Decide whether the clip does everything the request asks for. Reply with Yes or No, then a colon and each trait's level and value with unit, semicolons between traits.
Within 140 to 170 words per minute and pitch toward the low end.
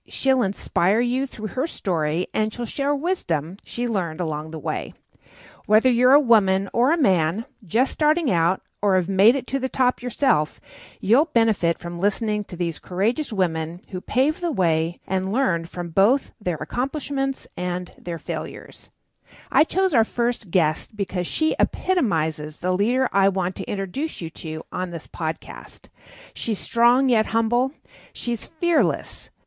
No: average, 160 wpm; high, 210 Hz